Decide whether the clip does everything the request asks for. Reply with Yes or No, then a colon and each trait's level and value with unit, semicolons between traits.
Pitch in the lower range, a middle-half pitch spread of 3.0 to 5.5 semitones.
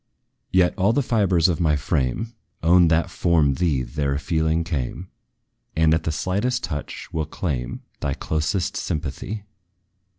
Yes: very low, 80 Hz; average, 3.6 semitones